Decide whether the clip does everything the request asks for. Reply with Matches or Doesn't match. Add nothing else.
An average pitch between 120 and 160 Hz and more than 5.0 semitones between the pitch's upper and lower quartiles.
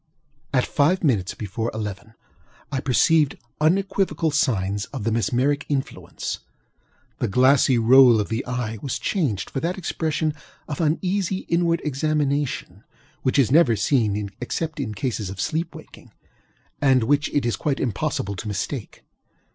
Matches